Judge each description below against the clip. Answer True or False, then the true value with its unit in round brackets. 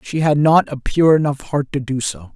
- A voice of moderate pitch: True (145 Hz)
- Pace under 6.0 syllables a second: True (4.9 syllables/s)